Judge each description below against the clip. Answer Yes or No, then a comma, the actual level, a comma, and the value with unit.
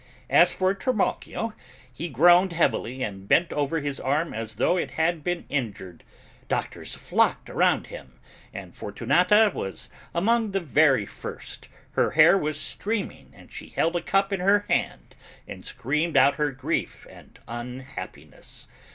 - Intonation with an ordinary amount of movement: No, wide, 6.1 semitones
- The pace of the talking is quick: No, average, 150 wpm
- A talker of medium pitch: Yes, medium, 160 Hz